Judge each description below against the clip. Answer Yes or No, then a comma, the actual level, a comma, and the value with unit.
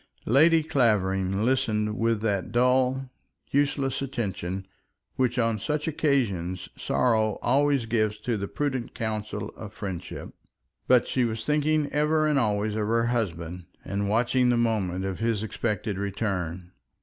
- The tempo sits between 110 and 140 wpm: Yes, slow, 135 wpm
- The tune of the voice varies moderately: Yes, average, 4.3 semitones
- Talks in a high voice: No, low, 115 Hz